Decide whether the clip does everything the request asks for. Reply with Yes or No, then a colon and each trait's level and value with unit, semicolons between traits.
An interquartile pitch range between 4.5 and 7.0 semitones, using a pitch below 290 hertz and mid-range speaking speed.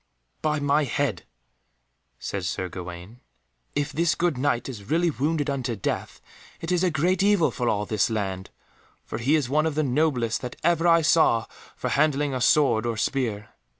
Yes: wide, 5.5 semitones; medium, 140 Hz; average, 180 wpm